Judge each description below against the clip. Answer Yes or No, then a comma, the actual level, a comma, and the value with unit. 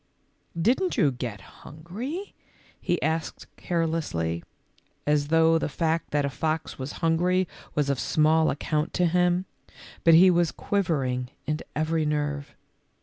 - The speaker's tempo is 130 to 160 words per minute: Yes, average, 145 wpm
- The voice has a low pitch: No, medium, 160 Hz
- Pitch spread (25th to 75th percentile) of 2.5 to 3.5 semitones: Yes, average, 2.9 semitones